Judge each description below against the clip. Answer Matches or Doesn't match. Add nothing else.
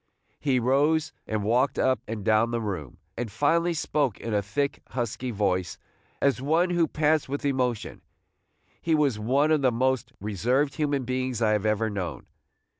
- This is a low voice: Matches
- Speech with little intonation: Doesn't match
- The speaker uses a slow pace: Doesn't match